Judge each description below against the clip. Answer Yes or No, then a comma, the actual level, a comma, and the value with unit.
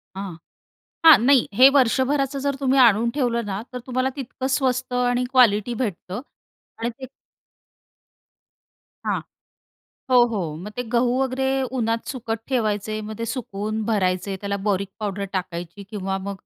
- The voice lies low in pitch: No, high, 230 Hz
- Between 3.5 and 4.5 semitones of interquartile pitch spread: Yes, average, 4.1 semitones